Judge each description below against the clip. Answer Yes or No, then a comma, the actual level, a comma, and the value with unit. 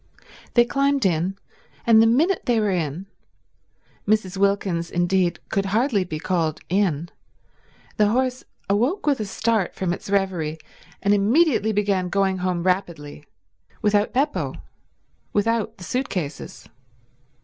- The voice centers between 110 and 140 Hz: No, high, 200 Hz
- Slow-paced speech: Yes, slow, 125 wpm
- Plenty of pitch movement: No, average, 4.0 semitones